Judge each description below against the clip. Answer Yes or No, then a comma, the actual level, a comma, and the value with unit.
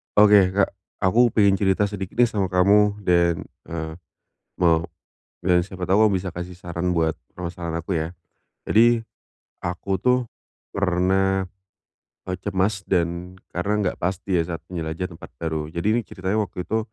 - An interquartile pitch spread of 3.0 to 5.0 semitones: No, narrow, 2.6 semitones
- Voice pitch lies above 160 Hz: No, very low, 90 Hz